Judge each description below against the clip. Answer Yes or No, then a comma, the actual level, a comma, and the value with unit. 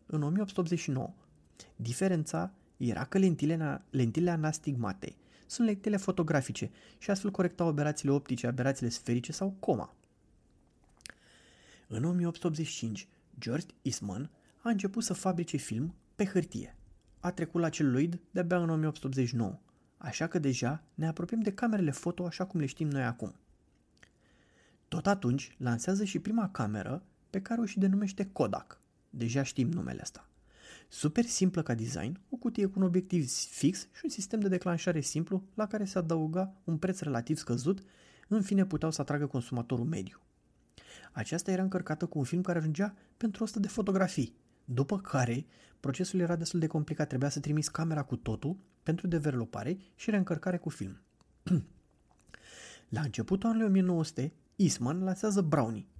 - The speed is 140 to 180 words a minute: Yes, average, 150 wpm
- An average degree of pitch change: No, wide, 6.0 semitones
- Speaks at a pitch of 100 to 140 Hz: No, medium, 160 Hz